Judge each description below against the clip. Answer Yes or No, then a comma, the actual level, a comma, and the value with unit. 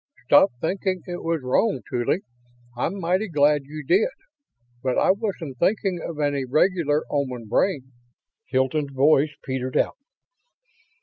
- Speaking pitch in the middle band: Yes, medium, 150 Hz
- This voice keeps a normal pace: No, slow, 130 wpm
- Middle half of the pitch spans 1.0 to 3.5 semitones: No, wide, 5.6 semitones